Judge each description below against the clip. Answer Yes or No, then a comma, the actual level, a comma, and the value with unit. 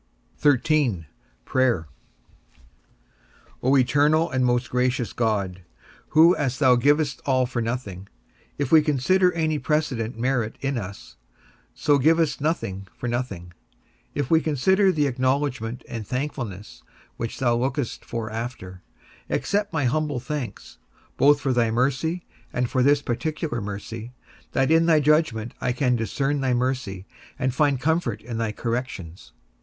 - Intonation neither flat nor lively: Yes, average, 4.2 semitones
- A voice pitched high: No, low, 130 Hz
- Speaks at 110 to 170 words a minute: Yes, average, 140 wpm